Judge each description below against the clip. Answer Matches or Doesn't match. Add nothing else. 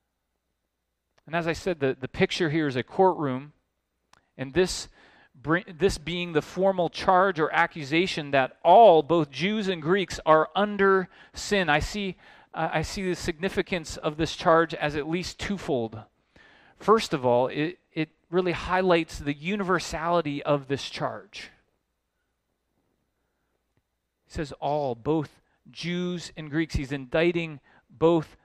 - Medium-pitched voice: Matches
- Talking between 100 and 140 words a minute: Matches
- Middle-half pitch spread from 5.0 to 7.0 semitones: Doesn't match